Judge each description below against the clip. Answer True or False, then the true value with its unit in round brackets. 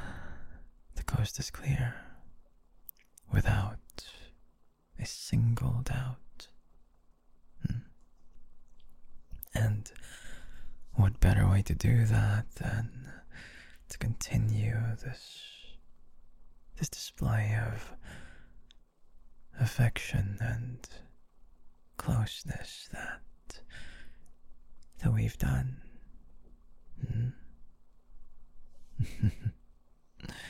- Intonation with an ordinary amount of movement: False (6.0 semitones)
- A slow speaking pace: True (60 wpm)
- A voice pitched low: True (80 Hz)